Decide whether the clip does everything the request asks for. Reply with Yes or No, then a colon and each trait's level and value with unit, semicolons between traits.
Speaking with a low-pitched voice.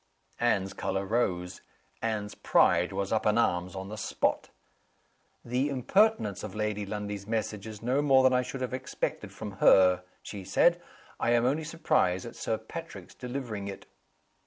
Yes: low, 110 Hz